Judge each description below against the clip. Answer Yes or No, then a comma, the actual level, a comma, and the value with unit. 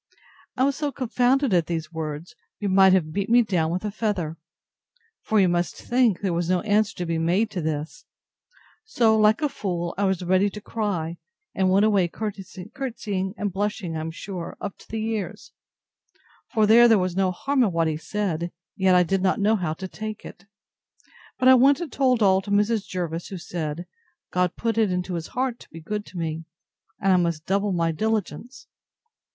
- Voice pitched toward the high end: Yes, high, 195 Hz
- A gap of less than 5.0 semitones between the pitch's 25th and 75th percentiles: Yes, average, 4.0 semitones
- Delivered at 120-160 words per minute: No, average, 200 wpm